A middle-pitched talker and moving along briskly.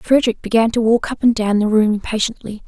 No: high, 225 Hz; fast, 225 wpm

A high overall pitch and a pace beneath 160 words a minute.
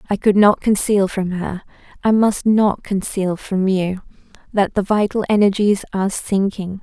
Yes: high, 200 Hz; average, 140 wpm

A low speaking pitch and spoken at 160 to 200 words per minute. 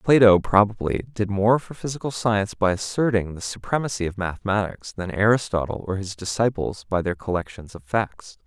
Yes: low, 105 Hz; average, 165 wpm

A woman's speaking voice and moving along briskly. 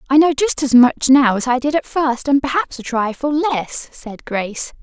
Yes: female; fast, 225 wpm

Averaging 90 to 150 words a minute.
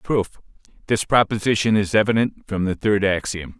Yes: slow, 135 wpm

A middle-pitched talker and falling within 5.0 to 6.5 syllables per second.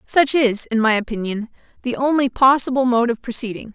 No: high, 245 Hz; 5.5 syllables/s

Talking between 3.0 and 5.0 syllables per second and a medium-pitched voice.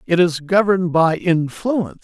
Yes: 4.8 syllables/s; medium, 175 Hz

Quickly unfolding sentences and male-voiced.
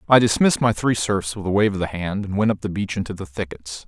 Yes: fast, 295 wpm; male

